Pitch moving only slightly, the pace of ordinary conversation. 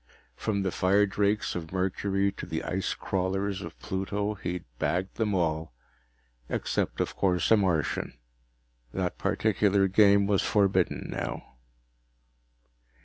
No: narrow, 1.8 semitones; slow, 120 wpm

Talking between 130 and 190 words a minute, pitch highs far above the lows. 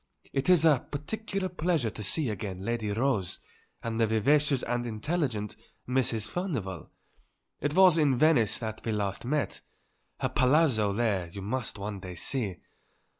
Yes: average, 150 wpm; wide, 6.0 semitones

